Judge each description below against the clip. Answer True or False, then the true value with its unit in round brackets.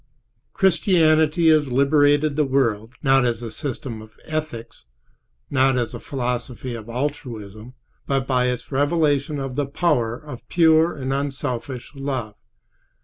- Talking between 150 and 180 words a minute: False (135 wpm)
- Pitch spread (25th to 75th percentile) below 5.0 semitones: True (3.4 semitones)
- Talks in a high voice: False (135 Hz)